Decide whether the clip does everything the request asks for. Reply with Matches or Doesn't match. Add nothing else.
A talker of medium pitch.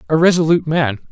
Matches